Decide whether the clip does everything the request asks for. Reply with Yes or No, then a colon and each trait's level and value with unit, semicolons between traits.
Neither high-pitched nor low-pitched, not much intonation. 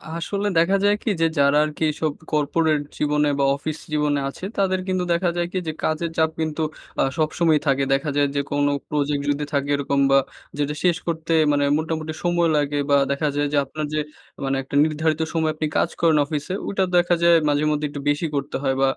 Yes: medium, 150 Hz; narrow, 2.3 semitones